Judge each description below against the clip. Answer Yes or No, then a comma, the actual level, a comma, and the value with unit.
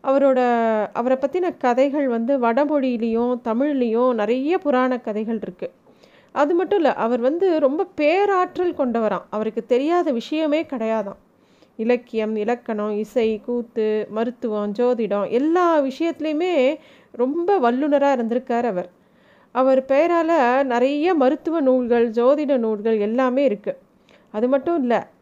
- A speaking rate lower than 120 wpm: Yes, average, 110 wpm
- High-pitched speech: Yes, very high, 255 Hz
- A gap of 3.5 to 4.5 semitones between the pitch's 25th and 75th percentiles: Yes, average, 4.2 semitones